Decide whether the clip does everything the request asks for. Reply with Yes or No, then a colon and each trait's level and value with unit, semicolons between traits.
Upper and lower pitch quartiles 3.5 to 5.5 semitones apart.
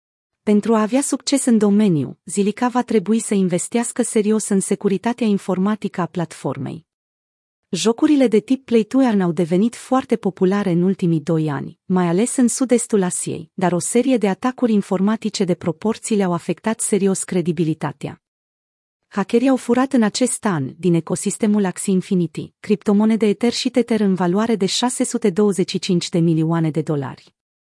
Yes: average, 4.4 semitones